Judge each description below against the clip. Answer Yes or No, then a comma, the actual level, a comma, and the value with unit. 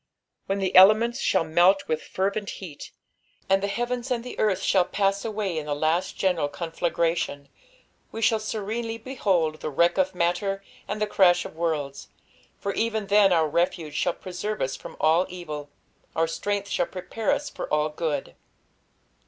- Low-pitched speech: No, medium, 185 Hz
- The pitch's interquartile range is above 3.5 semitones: Yes, average, 4.1 semitones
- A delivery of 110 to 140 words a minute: No, average, 170 wpm